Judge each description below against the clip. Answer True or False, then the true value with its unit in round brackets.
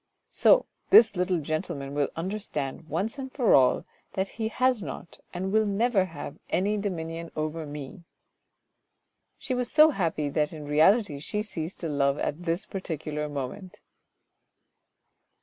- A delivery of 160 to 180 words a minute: False (145 wpm)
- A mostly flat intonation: False (5.3 semitones)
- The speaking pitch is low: False (170 Hz)